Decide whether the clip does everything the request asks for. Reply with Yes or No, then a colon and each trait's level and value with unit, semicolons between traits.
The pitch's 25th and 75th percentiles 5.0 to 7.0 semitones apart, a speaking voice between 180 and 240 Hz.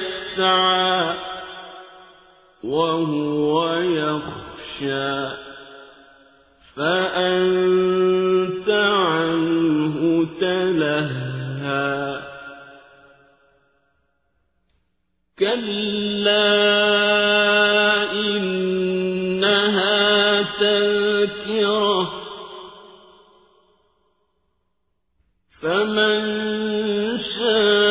Yes: wide, 5.4 semitones; medium, 185 Hz